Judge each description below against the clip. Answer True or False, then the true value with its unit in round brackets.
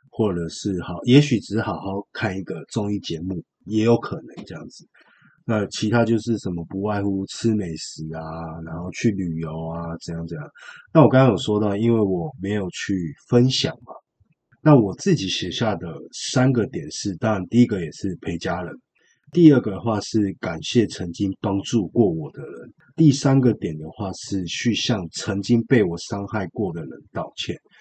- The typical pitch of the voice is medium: False (105 Hz)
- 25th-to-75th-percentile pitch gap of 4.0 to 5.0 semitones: True (4.3 semitones)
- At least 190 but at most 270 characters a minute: True (260 characters per minute)